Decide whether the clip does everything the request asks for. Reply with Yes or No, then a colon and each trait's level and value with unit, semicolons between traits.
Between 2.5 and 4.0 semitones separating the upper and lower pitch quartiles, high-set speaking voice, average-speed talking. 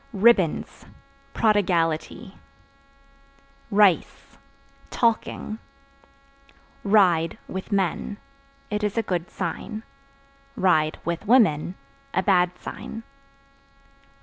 No: average, 3.7 semitones; high, 195 Hz; slow, 70 wpm